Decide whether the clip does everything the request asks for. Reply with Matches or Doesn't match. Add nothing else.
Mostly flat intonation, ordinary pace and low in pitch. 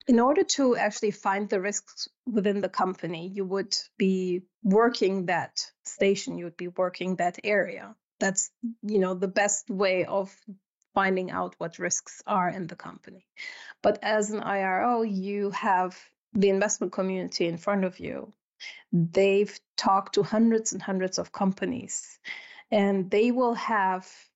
Doesn't match